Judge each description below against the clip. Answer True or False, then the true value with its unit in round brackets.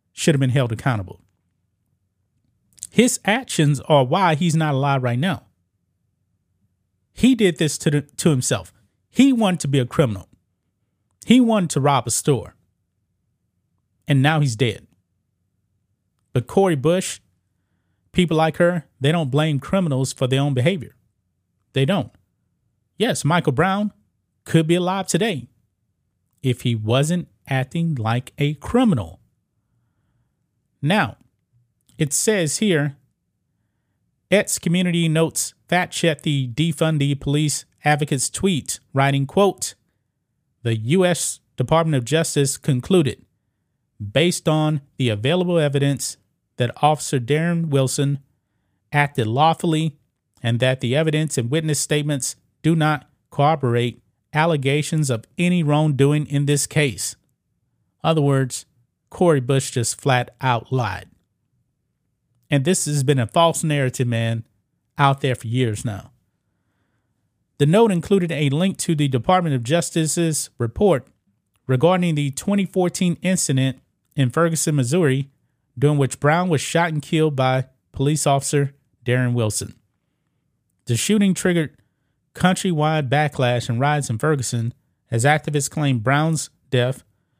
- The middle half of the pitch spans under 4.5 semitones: False (5.1 semitones)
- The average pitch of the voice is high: False (140 Hz)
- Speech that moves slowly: True (125 wpm)